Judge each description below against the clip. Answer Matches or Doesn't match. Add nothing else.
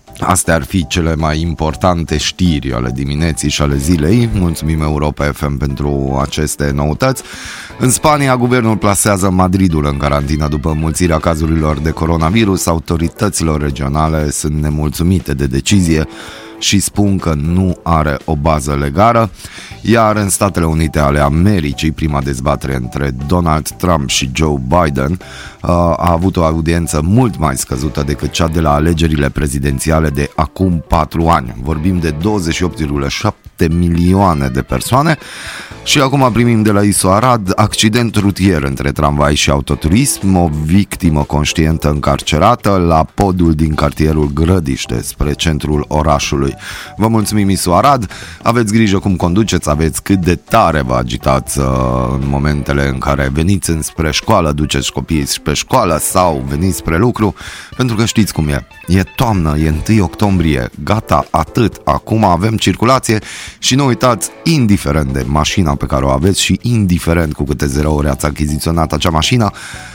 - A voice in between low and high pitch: Doesn't match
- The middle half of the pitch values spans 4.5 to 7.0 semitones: Matches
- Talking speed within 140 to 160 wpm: Matches